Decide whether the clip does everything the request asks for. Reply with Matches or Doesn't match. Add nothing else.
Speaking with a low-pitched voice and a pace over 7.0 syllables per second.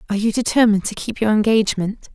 Doesn't match